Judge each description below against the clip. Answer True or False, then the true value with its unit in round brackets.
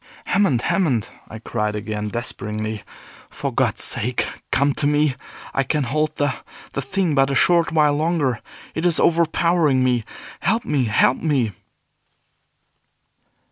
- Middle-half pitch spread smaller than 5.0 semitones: False (5.3 semitones)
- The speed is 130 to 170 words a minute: True (140 wpm)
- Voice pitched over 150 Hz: False (140 Hz)